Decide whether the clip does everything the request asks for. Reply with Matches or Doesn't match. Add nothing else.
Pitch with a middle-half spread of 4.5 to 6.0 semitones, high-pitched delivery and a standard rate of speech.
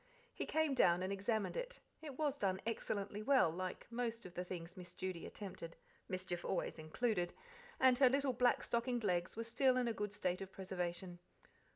Matches